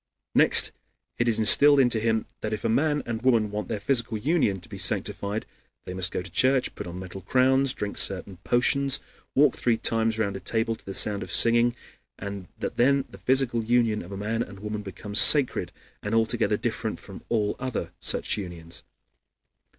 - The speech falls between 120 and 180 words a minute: No, average, 190 wpm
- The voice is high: No, low, 110 Hz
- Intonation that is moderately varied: Yes, average, 3.4 semitones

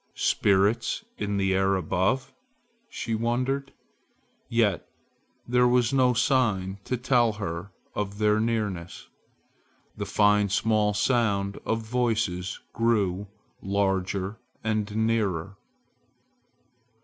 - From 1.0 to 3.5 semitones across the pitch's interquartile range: Yes, average, 3.2 semitones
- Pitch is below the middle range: Yes, low, 105 Hz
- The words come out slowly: Yes, slow, 100 wpm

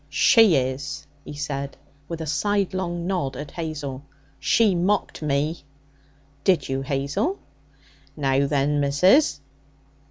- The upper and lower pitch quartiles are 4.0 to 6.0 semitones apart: Yes, average, 4.3 semitones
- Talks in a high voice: No, medium, 150 Hz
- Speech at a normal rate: No, slow, 115 wpm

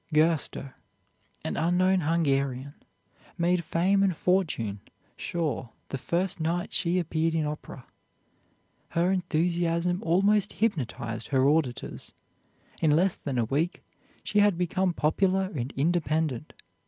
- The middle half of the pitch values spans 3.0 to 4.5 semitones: Yes, average, 3.5 semitones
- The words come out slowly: Yes, slow, 115 wpm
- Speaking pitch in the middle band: Yes, medium, 165 Hz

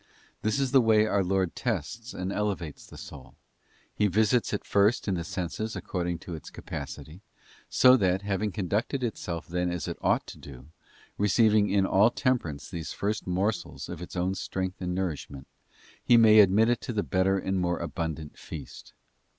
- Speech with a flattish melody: No, average, 3.5 semitones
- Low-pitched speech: Yes, very low, 95 Hz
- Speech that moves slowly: No, average, 175 wpm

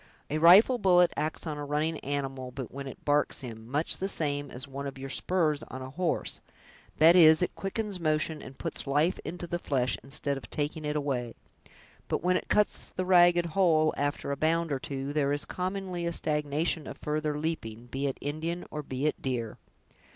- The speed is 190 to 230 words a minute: Yes, average, 195 wpm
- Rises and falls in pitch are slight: No, average, 3.5 semitones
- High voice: No, medium, 150 Hz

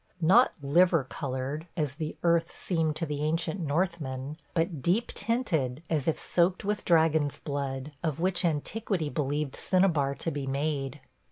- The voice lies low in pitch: No, medium, 155 Hz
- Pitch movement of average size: Yes, average, 3.4 semitones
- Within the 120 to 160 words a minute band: Yes, average, 150 wpm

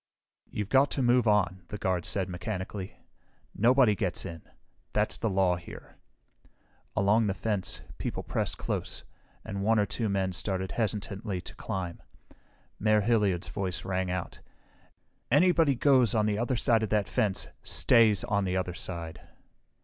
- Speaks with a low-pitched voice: Yes, low, 100 Hz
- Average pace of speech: Yes, average, 155 wpm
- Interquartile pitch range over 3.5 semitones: No, average, 3.2 semitones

